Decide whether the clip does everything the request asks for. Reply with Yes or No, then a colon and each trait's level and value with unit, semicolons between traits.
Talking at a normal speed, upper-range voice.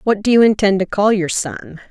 No: fast, 250 wpm; high, 200 Hz